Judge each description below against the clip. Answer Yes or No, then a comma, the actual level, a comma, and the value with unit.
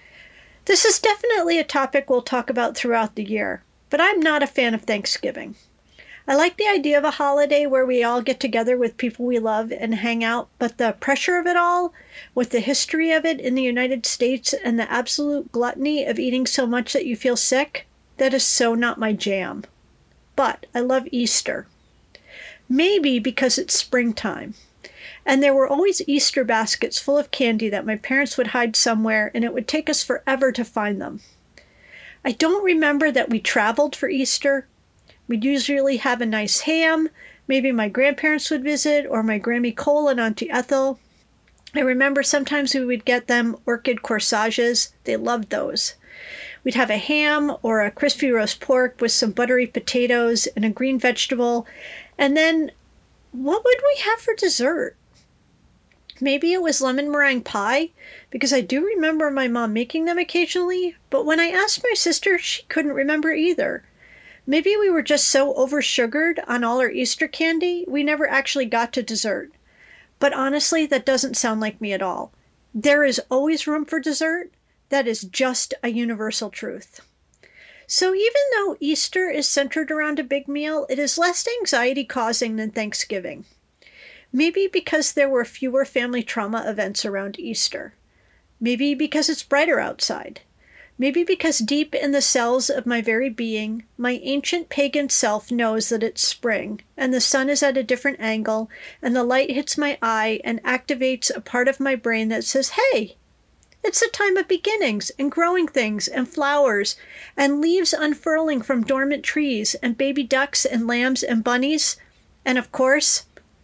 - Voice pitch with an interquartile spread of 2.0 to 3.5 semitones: No, average, 3.9 semitones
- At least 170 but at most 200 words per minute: Yes, average, 175 wpm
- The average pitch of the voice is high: Yes, very high, 270 Hz